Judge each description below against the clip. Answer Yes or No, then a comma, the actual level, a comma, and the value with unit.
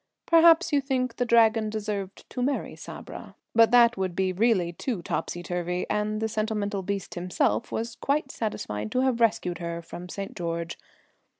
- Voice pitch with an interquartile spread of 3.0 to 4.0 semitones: No, average, 4.9 semitones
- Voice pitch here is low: No, high, 215 Hz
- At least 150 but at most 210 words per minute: Yes, average, 170 wpm